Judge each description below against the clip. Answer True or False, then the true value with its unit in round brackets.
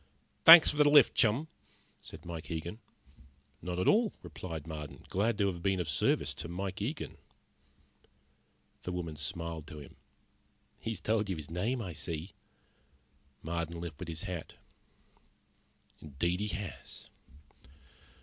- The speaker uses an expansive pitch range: False (4.5 semitones)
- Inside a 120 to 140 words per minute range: True (135 wpm)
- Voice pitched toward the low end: True (90 Hz)